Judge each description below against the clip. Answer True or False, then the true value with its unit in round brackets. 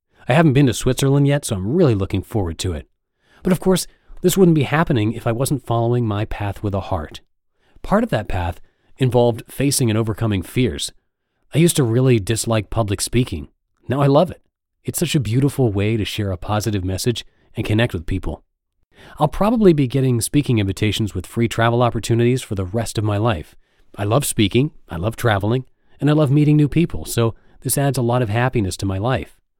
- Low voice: True (115 Hz)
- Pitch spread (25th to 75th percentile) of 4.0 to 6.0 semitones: True (5.0 semitones)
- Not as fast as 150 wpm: False (205 wpm)